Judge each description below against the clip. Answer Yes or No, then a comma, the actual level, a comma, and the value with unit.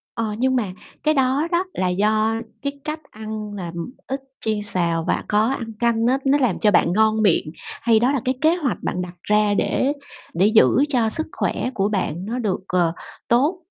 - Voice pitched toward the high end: Yes, high, 220 Hz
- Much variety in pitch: No, average, 4.3 semitones